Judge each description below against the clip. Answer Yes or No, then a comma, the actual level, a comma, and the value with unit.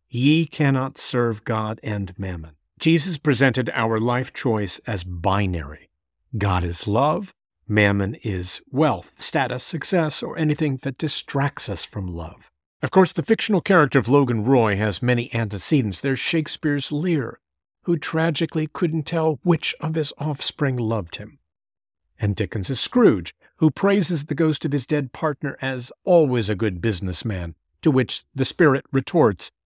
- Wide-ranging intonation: Yes, wide, 6.9 semitones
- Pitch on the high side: No, low, 130 Hz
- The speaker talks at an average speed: Yes, average, 150 wpm